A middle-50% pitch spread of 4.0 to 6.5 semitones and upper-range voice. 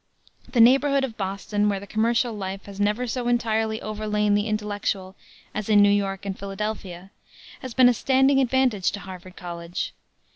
No: average, 3.2 semitones; high, 210 Hz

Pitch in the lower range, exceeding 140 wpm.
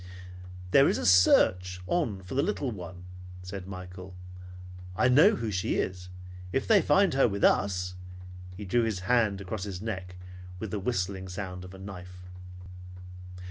Yes: very low, 95 Hz; average, 165 wpm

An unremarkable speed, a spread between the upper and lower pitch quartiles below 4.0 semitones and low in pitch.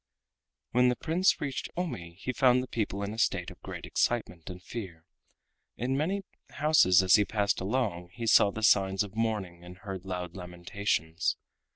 No: average, 175 wpm; average, 5.3 semitones; low, 100 Hz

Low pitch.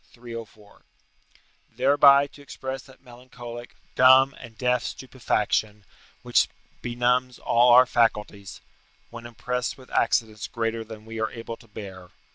Yes: low, 120 Hz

